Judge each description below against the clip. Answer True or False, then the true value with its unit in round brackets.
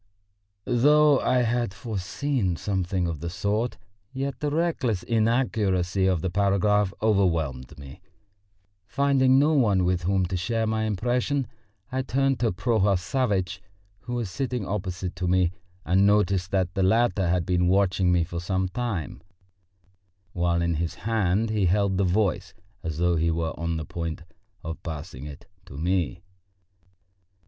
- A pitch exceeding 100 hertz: False (95 Hz)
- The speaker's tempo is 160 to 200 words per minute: False (150 wpm)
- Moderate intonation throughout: True (4.6 semitones)